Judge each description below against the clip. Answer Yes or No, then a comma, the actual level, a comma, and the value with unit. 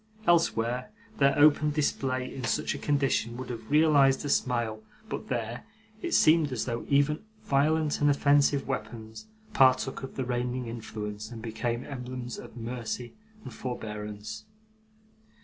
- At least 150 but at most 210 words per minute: No, average, 140 wpm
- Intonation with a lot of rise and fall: No, average, 3.6 semitones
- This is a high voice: No, low, 125 Hz